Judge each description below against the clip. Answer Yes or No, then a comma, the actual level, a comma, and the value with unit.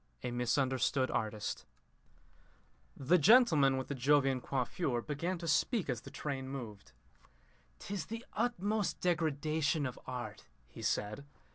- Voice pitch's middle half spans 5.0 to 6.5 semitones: Yes, average, 5.3 semitones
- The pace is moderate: No, slow, 125 wpm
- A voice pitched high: No, medium, 140 Hz